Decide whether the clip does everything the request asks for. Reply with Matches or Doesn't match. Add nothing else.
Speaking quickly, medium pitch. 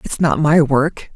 Matches